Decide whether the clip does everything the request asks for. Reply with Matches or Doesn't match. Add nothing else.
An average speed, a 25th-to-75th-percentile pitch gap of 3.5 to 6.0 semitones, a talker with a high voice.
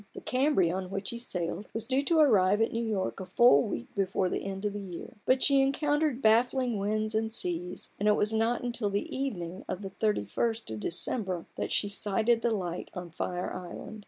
Doesn't match